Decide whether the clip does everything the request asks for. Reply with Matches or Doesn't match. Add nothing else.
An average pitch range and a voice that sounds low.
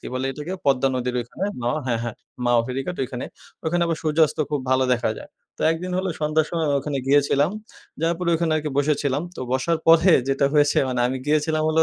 Doesn't match